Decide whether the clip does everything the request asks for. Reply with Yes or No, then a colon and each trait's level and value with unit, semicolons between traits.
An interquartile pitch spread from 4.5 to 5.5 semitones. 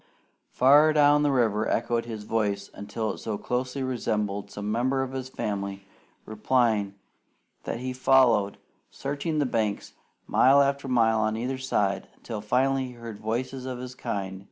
No: average, 3.8 semitones